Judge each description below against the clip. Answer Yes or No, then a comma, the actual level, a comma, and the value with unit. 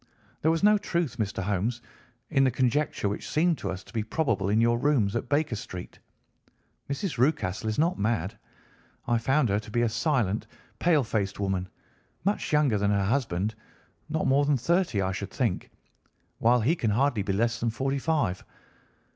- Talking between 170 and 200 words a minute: Yes, average, 180 wpm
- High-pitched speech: No, low, 120 Hz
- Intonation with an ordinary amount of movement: No, wide, 6.0 semitones